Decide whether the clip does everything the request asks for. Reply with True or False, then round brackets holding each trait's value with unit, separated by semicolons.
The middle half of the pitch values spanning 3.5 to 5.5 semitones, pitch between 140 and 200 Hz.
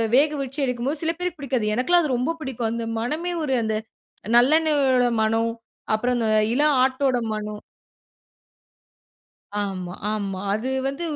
False (4.5 semitones; 255 Hz)